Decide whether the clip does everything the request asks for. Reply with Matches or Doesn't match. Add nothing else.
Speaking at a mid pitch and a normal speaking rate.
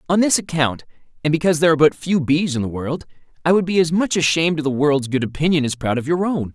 Doesn't match